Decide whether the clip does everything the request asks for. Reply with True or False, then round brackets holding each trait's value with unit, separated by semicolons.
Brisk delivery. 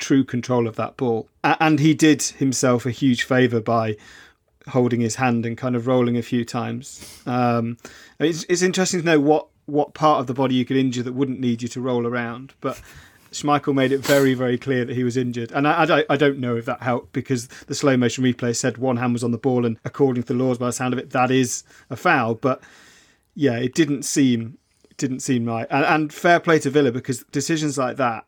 True (235 wpm)